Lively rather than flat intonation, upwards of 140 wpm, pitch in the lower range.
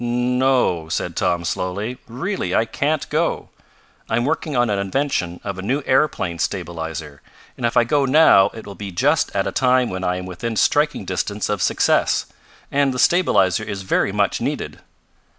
Yes: wide, 6.5 semitones; average, 175 wpm; low, 115 Hz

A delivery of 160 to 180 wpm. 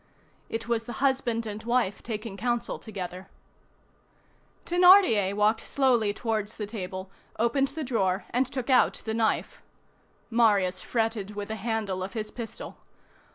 No: average, 140 wpm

